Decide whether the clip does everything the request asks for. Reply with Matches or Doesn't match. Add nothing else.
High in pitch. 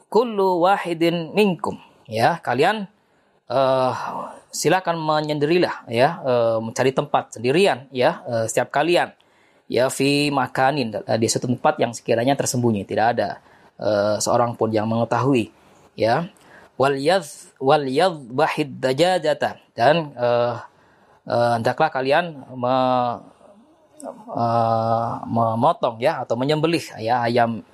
Doesn't match